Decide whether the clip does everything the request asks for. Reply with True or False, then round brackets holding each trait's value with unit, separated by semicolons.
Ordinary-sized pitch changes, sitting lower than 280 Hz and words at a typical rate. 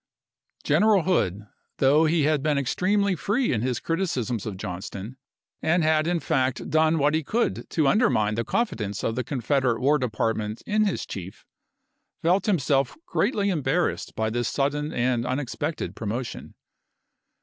False (6.2 semitones; 140 Hz; 150 wpm)